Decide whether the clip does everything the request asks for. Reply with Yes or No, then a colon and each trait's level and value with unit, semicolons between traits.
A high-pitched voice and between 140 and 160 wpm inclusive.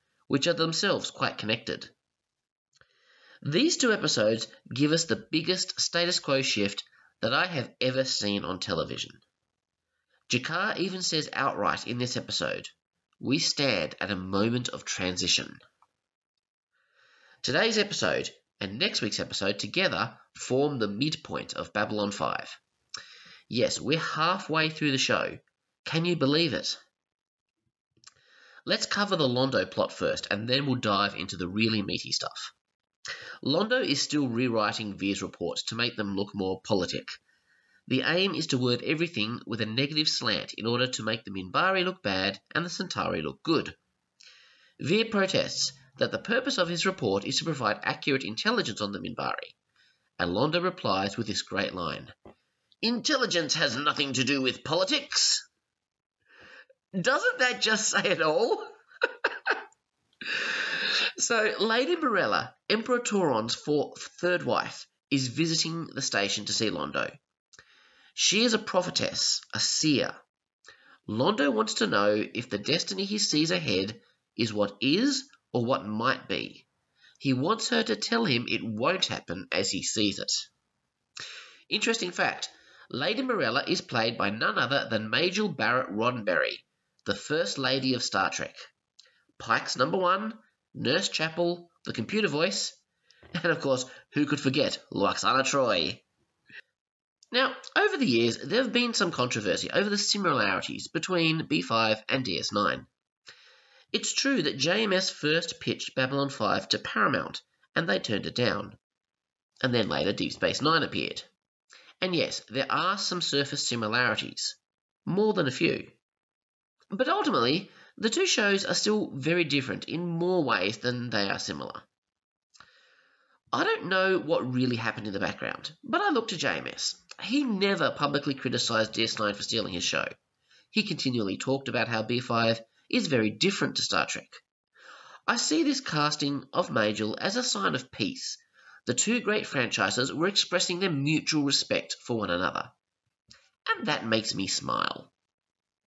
No: medium, 145 Hz; average, 150 wpm